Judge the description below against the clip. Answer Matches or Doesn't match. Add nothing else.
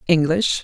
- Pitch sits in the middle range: Matches